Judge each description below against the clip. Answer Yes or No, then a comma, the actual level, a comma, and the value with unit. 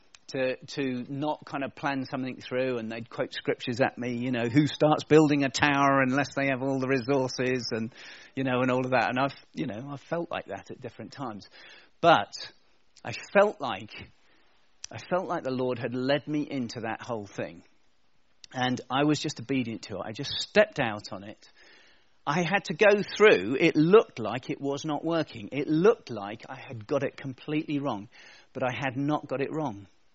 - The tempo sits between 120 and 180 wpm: No, fast, 205 wpm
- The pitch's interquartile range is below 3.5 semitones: Yes, average, 2.9 semitones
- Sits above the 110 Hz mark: Yes, low, 135 Hz